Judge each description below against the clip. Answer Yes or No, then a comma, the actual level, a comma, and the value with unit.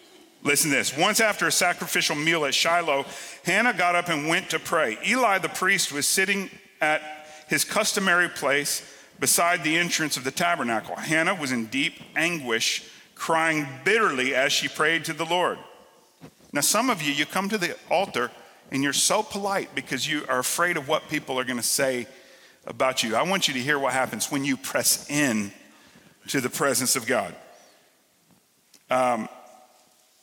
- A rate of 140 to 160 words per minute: No, average, 175 wpm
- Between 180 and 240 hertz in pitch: No, medium, 155 Hz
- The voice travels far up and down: No, average, 4.8 semitones